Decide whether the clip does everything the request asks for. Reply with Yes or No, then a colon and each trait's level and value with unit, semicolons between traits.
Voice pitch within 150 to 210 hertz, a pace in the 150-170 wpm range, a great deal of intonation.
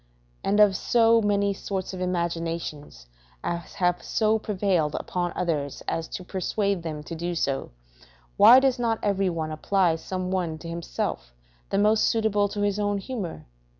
No: medium, 185 Hz; average, 160 wpm; average, 3.6 semitones